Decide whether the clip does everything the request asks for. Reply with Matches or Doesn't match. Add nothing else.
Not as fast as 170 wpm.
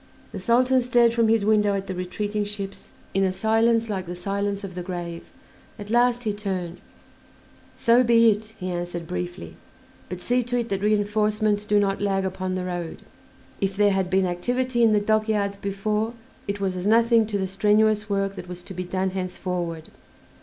Doesn't match